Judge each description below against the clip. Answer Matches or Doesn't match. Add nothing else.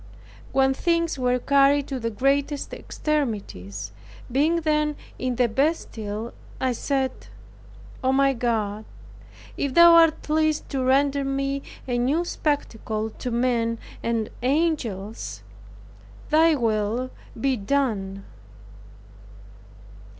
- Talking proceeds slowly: Matches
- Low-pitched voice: Doesn't match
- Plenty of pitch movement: Doesn't match